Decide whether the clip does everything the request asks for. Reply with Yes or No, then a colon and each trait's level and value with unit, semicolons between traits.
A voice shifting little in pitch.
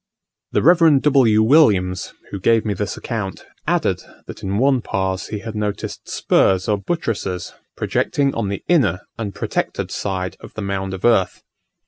No: average, 3.9 semitones